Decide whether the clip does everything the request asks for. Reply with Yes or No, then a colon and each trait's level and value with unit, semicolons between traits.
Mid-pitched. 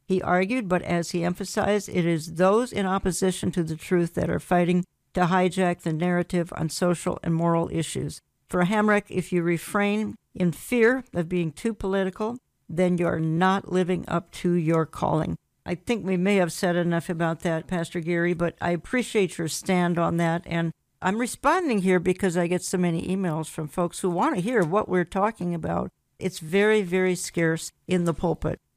Yes: medium, 180 Hz